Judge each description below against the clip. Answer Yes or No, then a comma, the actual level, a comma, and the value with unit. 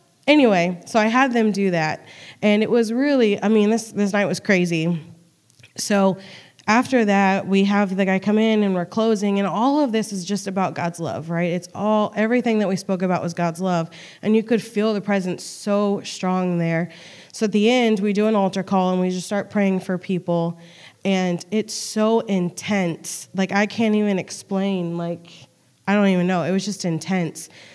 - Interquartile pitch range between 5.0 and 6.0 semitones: No, average, 3.3 semitones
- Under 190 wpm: No, average, 200 wpm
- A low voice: No, high, 195 Hz